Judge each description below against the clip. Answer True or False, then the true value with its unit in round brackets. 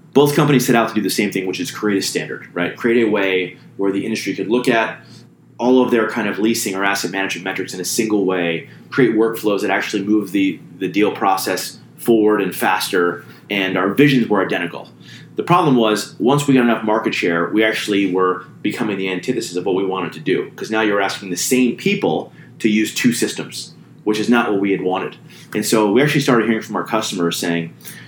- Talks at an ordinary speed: False (220 wpm)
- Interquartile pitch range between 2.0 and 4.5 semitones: True (3.9 semitones)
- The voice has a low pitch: True (105 Hz)